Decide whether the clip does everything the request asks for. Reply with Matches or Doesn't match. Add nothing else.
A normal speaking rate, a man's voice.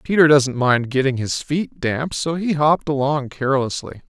Matches